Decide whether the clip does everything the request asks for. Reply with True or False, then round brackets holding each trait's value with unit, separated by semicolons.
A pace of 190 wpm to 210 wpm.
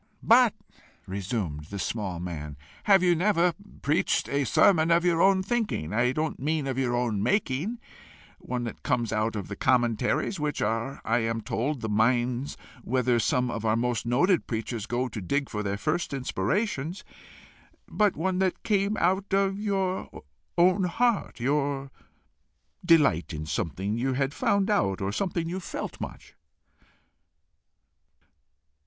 False (150 wpm)